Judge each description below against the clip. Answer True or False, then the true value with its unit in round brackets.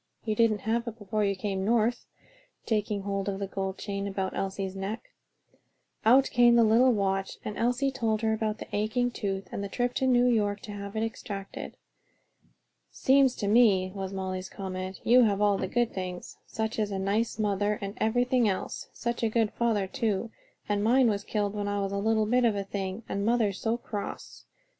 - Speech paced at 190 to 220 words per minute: True (195 wpm)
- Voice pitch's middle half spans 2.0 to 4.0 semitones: True (2.8 semitones)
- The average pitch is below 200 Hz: False (210 Hz)